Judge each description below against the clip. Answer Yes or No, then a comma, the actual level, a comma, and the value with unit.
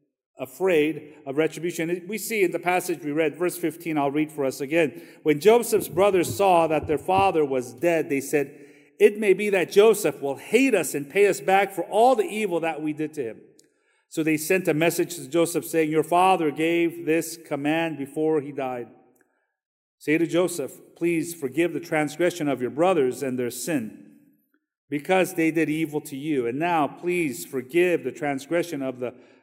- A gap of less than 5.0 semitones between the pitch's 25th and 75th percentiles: Yes, average, 3.5 semitones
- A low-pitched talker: No, medium, 160 Hz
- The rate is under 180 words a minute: No, average, 190 wpm